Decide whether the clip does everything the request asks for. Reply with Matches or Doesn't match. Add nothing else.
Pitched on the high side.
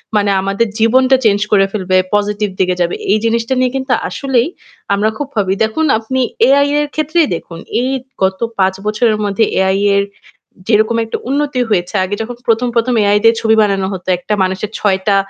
Matches